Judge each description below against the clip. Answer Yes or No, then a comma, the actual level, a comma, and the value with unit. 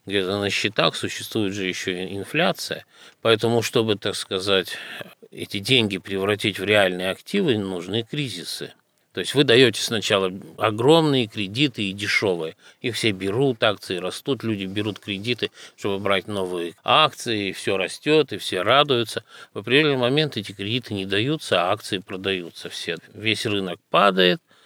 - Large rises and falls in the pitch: No, average, 3.5 semitones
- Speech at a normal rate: Yes, average, 150 wpm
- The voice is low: Yes, low, 100 Hz